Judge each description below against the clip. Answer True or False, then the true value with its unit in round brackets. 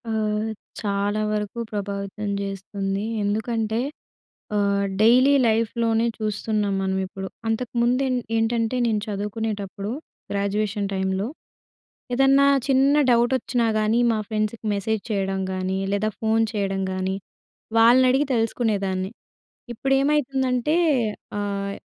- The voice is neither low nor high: False (215 Hz)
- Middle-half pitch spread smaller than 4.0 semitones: True (2.8 semitones)